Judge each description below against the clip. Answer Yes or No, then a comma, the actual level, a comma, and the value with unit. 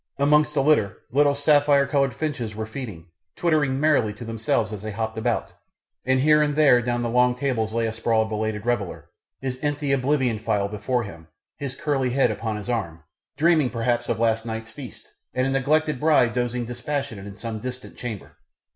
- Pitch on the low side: Yes, low, 125 Hz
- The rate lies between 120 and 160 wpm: No, average, 185 wpm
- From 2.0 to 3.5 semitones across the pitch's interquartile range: No, average, 4.1 semitones